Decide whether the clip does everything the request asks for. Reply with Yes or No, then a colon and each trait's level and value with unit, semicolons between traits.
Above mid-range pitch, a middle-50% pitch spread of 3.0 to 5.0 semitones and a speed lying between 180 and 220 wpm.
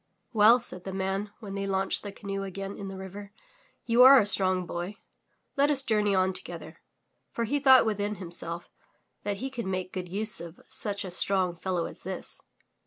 No: high, 195 Hz; narrow, 2.4 semitones; average, 190 wpm